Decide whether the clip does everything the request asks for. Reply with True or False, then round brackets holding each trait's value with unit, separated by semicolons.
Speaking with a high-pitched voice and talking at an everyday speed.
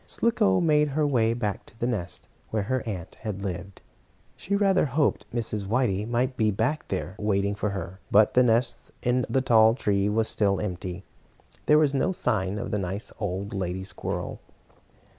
False (110 Hz; 180 wpm)